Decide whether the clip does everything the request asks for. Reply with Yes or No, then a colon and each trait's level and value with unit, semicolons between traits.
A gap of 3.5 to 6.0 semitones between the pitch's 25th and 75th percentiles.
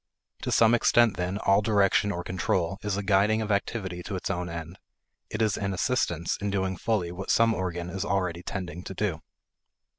No: average, 2.7 semitones